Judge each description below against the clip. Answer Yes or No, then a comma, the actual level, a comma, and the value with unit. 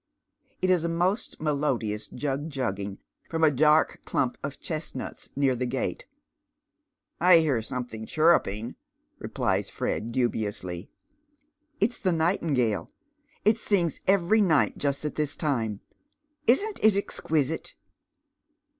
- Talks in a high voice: No, medium, 150 Hz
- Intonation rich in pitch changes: Yes, wide, 6.0 semitones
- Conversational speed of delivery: No, slow, 130 wpm